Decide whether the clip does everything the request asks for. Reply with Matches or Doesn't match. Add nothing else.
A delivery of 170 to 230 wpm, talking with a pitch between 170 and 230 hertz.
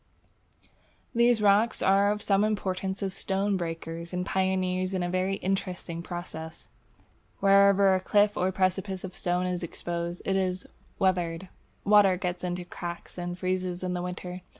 Doesn't match